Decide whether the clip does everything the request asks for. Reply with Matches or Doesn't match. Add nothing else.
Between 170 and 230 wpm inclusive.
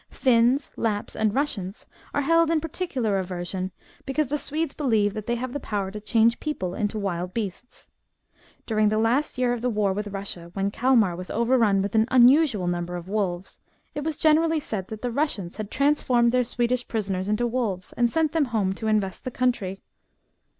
Matches